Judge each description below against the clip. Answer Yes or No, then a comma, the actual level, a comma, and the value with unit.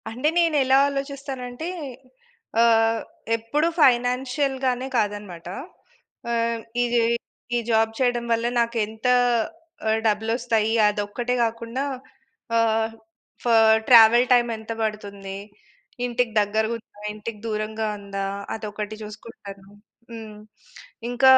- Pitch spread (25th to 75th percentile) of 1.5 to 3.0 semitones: Yes, narrow, 2.4 semitones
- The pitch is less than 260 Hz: Yes, high, 230 Hz